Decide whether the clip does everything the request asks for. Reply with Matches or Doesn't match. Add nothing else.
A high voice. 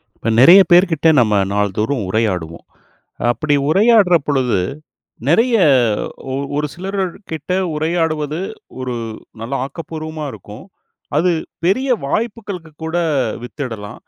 Doesn't match